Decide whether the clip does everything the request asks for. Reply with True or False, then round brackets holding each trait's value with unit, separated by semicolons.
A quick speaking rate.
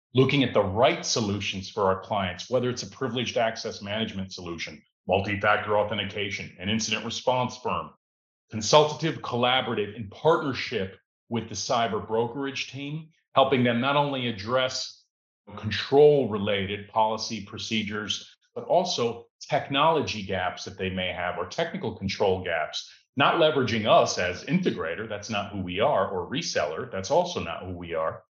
False (145 wpm)